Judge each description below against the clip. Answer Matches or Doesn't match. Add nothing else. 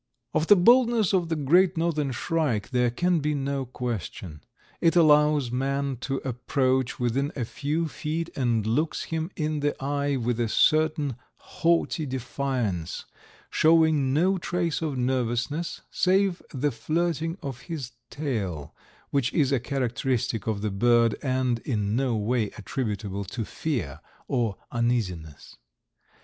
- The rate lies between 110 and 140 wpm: Matches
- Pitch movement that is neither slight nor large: Matches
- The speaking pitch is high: Doesn't match